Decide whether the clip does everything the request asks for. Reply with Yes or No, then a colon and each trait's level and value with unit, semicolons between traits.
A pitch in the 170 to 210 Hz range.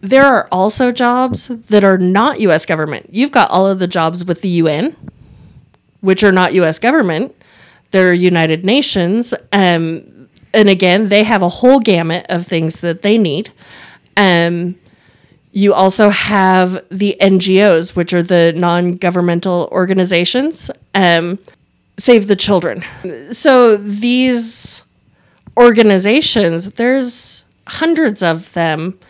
Yes: high, 190 Hz